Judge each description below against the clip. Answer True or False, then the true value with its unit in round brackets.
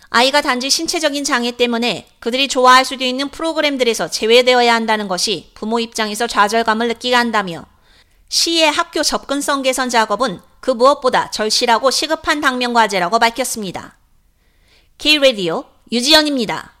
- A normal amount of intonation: True (3.4 semitones)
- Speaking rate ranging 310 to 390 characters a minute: True (365 characters per minute)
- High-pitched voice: True (250 Hz)